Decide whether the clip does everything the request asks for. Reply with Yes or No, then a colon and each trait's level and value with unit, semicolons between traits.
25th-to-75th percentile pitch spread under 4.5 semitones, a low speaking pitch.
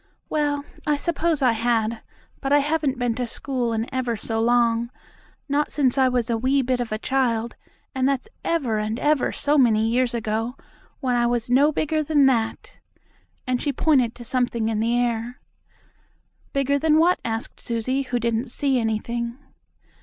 No: average, 3.2 semitones; high, 245 Hz